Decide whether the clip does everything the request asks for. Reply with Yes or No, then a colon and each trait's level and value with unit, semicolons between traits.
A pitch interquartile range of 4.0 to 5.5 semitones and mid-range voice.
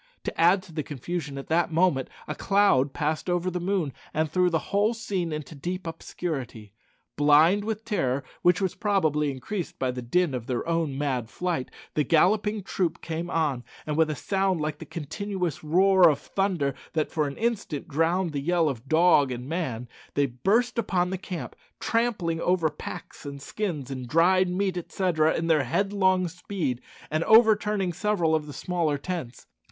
Yes: average, 4.4 semitones; medium, 165 Hz